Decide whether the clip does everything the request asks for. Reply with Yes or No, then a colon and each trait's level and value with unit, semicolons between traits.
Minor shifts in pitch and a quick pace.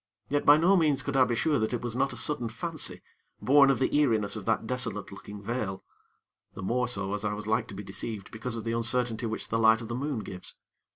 No: average, 3.8 semitones; fast, 245 wpm